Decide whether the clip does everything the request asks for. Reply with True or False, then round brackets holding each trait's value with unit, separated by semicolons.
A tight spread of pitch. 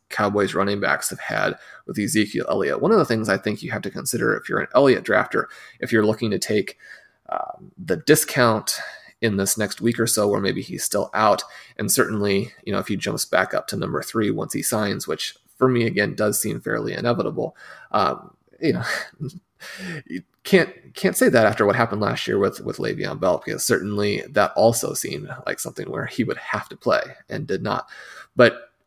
True (2.2 semitones)